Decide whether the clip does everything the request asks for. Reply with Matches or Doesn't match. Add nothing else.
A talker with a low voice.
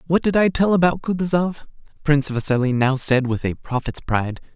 Doesn't match